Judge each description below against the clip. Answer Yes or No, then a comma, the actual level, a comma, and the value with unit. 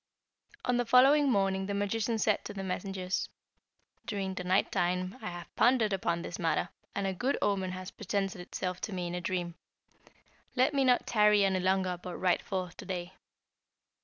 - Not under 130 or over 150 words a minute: No, average, 185 wpm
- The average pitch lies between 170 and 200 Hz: Yes, high, 190 Hz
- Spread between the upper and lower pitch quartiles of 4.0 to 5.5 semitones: No, narrow, 2.5 semitones